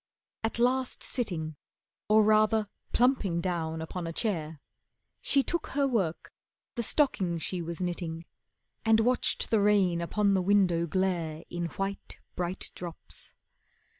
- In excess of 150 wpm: No, slow, 135 wpm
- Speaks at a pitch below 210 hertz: Yes, medium, 185 Hz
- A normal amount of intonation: Yes, average, 4.4 semitones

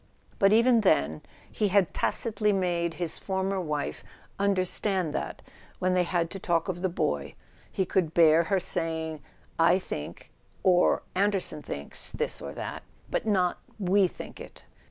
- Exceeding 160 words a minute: No, average, 155 wpm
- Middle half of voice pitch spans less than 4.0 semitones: Yes, average, 3.0 semitones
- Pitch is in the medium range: Yes, medium, 180 Hz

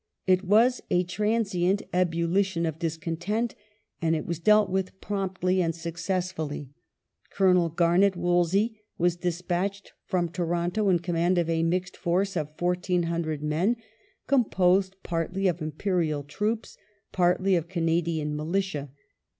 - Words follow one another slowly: Yes, slow, 125 wpm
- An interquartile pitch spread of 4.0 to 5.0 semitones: No, narrow, 2.5 semitones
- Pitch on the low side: No, medium, 175 Hz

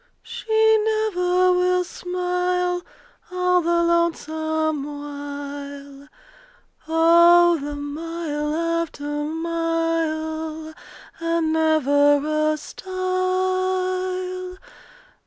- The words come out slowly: Yes, slow, 65 wpm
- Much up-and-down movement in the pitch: No, average, 2.9 semitones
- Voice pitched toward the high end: Yes, very high, 330 Hz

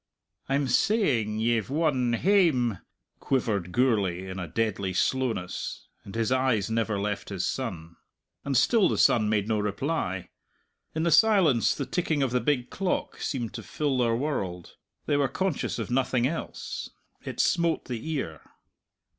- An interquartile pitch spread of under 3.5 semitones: No, wide, 5.5 semitones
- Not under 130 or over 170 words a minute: Yes, average, 155 wpm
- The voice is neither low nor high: No, low, 120 Hz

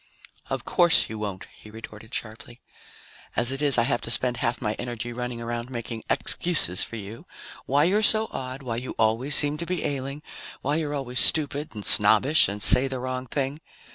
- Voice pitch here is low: Yes, low, 125 Hz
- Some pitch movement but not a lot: Yes, average, 3.8 semitones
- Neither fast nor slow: Yes, average, 195 wpm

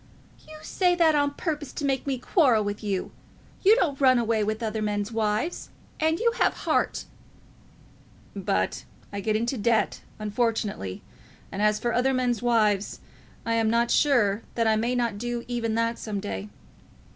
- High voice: Yes, high, 230 Hz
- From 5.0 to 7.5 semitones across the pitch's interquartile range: No, average, 3.8 semitones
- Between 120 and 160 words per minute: No, average, 170 wpm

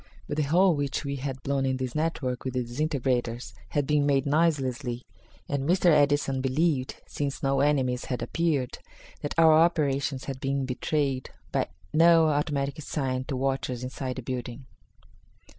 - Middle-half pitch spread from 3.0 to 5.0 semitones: No, narrow, 2.5 semitones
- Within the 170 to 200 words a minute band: No, average, 160 wpm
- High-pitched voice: No, medium, 140 Hz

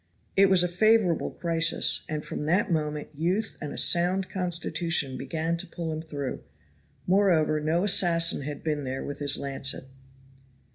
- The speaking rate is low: No, average, 155 wpm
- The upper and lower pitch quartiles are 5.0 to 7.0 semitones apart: No, average, 3.0 semitones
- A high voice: No, medium, 165 Hz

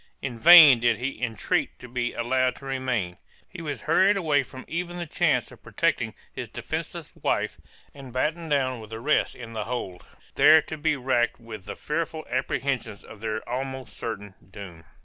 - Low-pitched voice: Yes, low, 130 Hz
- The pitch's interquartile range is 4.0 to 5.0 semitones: Yes, average, 4.6 semitones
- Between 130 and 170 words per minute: No, average, 180 wpm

